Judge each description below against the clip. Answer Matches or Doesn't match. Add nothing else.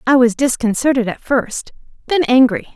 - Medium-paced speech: Matches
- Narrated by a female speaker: Matches